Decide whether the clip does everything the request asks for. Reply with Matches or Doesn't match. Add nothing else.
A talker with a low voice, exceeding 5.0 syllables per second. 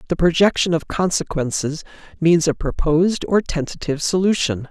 Doesn't match